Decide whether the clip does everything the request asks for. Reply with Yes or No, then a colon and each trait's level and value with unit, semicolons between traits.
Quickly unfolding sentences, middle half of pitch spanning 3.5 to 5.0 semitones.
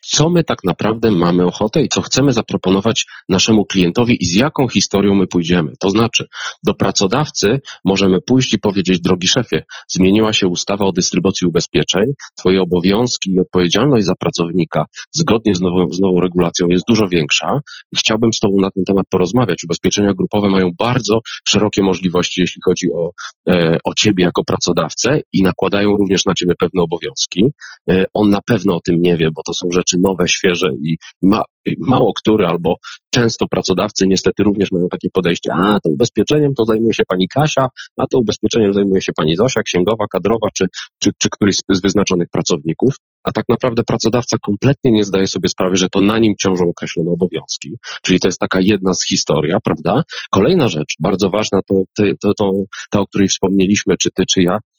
No: fast, 185 wpm; average, 2.7 semitones